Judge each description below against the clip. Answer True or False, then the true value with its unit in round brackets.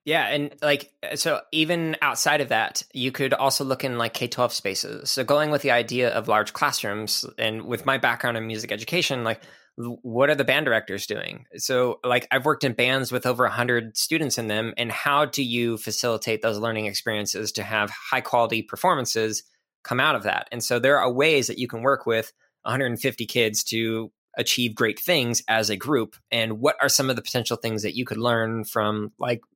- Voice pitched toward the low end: True (120 Hz)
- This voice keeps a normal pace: False (215 wpm)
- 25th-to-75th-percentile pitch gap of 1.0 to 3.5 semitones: True (3.1 semitones)